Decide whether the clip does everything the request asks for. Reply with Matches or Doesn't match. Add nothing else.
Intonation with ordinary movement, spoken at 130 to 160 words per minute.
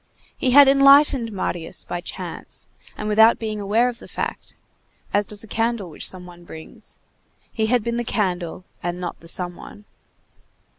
Doesn't match